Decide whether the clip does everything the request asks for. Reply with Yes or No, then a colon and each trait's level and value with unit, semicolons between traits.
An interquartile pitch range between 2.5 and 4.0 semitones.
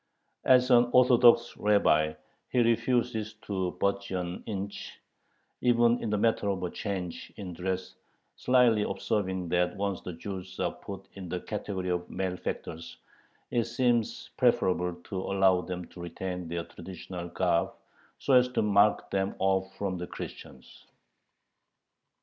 Yes: average, 3.6 semitones